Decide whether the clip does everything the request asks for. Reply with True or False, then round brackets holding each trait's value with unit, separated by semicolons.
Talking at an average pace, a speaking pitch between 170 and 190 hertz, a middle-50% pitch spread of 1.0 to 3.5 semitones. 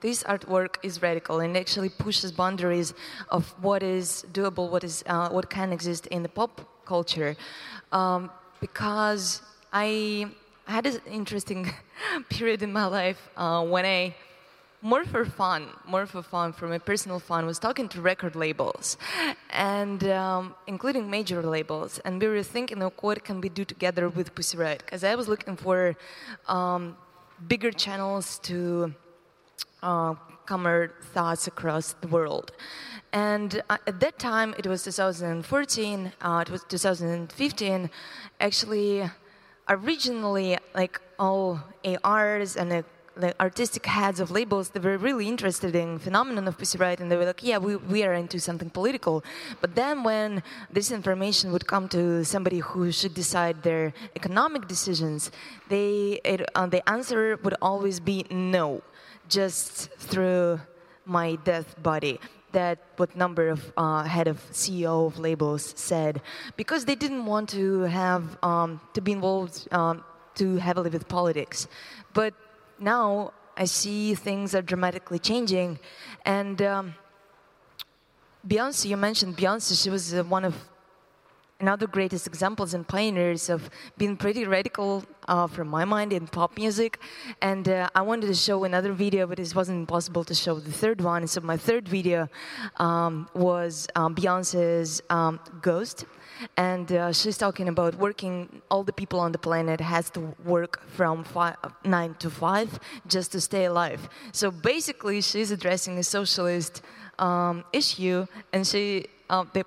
True (150 wpm; 185 Hz; 2.7 semitones)